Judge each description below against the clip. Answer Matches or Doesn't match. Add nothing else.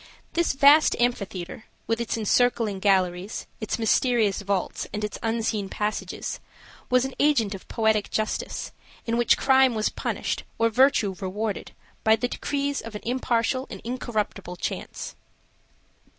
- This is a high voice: Matches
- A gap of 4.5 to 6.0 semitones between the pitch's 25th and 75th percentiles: Doesn't match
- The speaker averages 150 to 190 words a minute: Doesn't match